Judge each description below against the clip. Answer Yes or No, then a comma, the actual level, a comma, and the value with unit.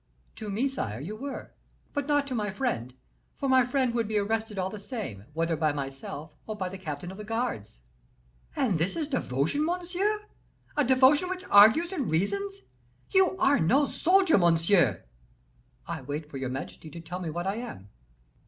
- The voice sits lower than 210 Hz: No, high, 215 Hz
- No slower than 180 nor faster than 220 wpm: Yes, average, 185 wpm